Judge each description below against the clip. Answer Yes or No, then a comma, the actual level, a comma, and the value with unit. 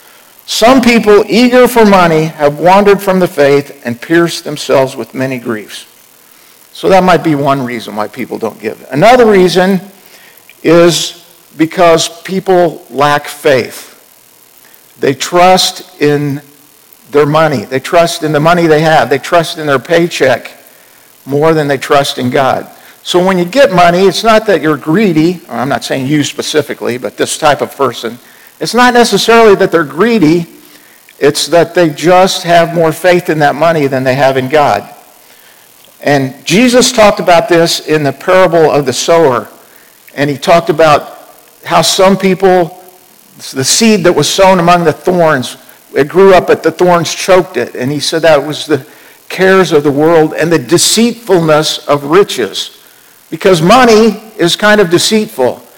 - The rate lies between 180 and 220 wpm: No, average, 165 wpm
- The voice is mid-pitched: Yes, medium, 170 Hz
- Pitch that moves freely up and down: No, average, 4.2 semitones